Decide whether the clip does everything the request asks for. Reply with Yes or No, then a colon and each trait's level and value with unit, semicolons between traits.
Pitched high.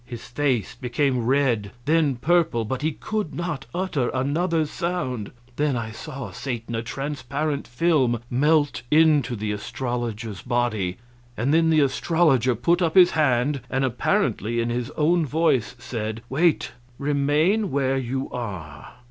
No: low, 135 Hz